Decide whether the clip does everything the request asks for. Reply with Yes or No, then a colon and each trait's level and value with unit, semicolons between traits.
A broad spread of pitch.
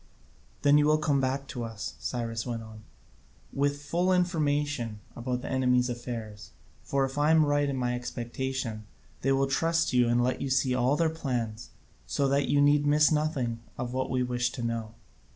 No: average, 3.3 semitones